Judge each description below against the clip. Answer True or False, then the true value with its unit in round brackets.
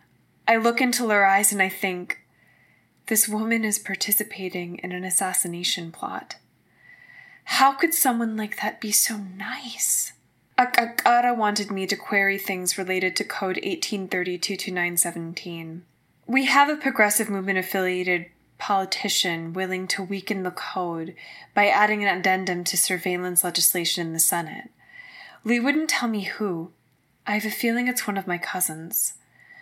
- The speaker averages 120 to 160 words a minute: True (140 wpm)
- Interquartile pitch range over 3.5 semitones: True (3.9 semitones)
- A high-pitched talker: True (195 Hz)